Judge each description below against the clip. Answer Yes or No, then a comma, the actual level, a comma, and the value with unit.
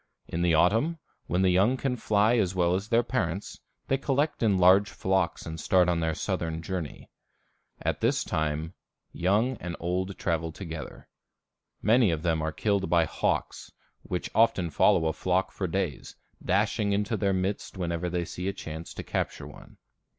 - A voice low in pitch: Yes, very low, 95 Hz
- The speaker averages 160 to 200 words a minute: Yes, average, 170 wpm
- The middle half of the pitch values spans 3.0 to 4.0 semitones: Yes, average, 3.6 semitones